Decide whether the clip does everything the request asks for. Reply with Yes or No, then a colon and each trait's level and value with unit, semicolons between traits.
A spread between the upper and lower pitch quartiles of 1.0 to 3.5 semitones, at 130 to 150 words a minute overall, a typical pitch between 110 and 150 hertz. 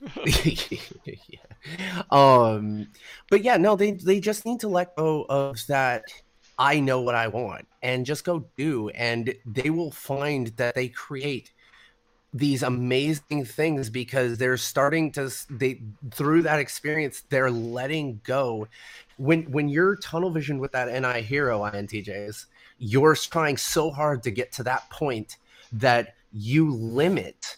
No: average, 4.2 semitones; average, 145 wpm; low, 135 Hz